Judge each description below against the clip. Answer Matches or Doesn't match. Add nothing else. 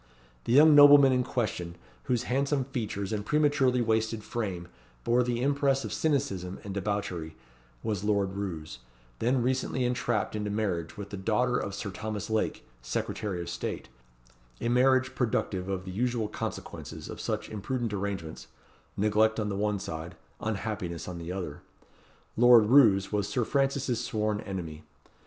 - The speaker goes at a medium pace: Matches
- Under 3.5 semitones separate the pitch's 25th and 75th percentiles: Doesn't match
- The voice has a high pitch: Doesn't match